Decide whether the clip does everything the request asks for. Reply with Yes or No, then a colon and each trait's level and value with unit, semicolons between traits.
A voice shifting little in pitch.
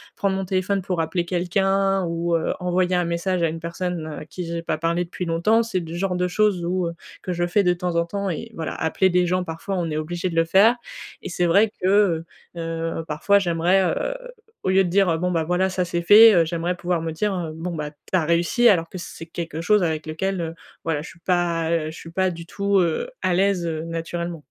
Yes: narrow, 2.2 semitones